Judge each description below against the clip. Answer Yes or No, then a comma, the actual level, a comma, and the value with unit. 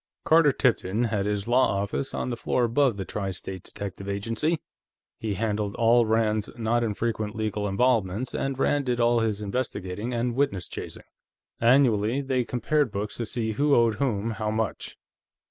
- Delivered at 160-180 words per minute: Yes, average, 165 wpm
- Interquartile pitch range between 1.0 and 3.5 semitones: Yes, average, 3.2 semitones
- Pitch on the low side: Yes, low, 115 Hz